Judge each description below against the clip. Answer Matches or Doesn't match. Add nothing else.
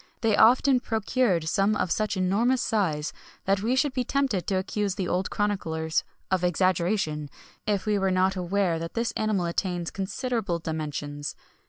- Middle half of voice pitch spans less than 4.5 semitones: Matches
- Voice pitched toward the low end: Doesn't match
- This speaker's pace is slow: Doesn't match